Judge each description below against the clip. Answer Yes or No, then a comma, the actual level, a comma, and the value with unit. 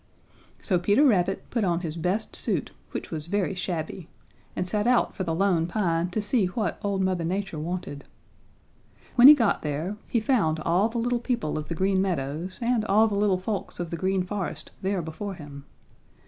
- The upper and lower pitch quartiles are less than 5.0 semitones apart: Yes, average, 3.8 semitones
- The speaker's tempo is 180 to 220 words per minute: Yes, average, 190 wpm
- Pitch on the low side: No, high, 190 Hz